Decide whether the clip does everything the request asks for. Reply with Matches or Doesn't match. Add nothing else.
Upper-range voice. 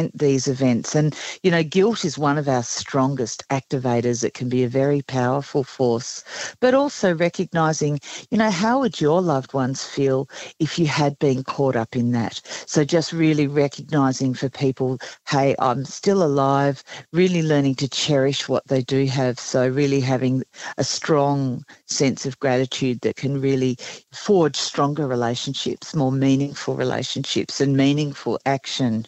Doesn't match